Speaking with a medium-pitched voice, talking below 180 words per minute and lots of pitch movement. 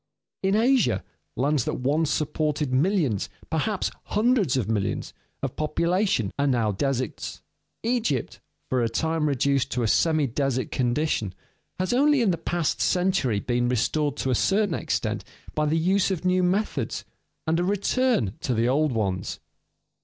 Yes: medium, 150 Hz; average, 155 wpm; wide, 6.8 semitones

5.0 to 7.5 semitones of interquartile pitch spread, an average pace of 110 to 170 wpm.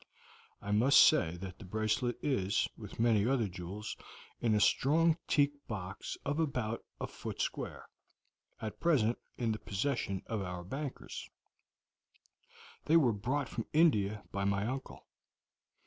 Yes: wide, 5.6 semitones; average, 140 wpm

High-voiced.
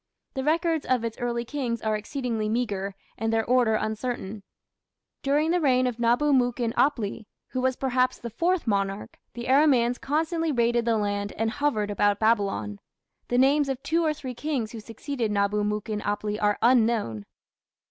Yes: high, 235 Hz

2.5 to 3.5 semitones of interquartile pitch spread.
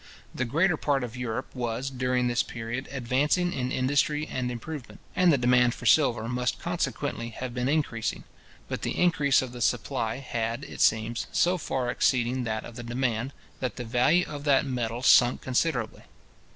Yes: average, 2.8 semitones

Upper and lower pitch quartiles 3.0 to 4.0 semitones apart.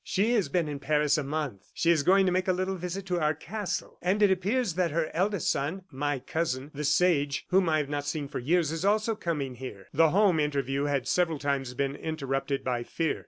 No: average, 4.4 semitones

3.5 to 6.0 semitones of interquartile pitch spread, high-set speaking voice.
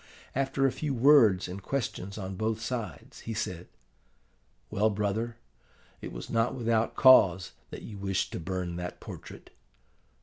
No: average, 4.0 semitones; low, 105 Hz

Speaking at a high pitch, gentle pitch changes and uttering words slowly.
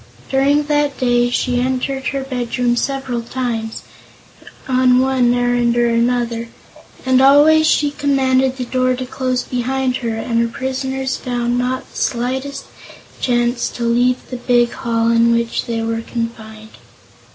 No: very high, 250 Hz; narrow, 1.8 semitones; average, 145 wpm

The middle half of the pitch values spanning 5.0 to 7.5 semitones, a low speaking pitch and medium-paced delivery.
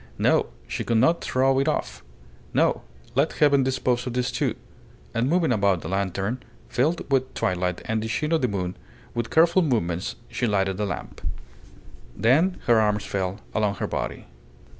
Yes: average, 5.3 semitones; low, 120 Hz; average, 170 wpm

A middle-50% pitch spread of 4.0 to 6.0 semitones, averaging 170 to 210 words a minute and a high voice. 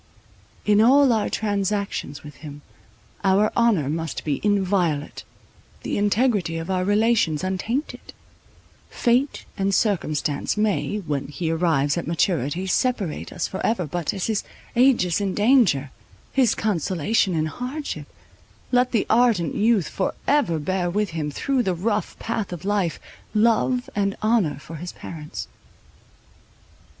No: average, 5.3 semitones; slow, 135 wpm; high, 195 Hz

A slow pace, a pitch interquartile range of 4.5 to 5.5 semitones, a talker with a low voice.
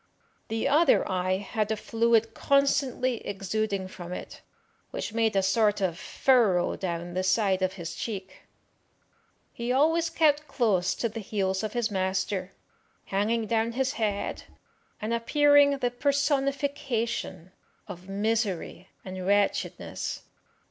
No: slow, 130 wpm; average, 5.0 semitones; high, 220 Hz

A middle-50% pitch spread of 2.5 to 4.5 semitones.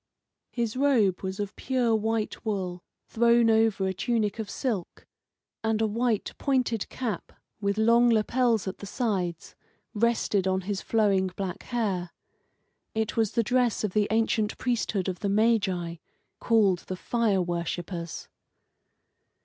Yes: average, 3.4 semitones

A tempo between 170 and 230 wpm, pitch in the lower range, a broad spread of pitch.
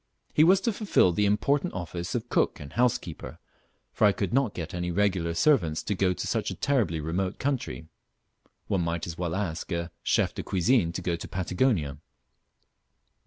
Yes: average, 180 wpm; very low, 90 Hz; wide, 6.1 semitones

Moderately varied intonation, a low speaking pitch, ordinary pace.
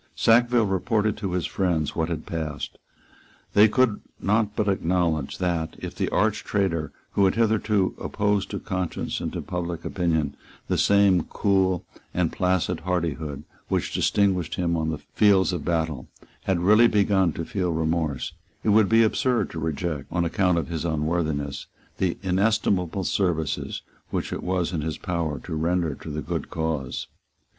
Yes: average, 3.6 semitones; very low, 90 Hz; average, 160 wpm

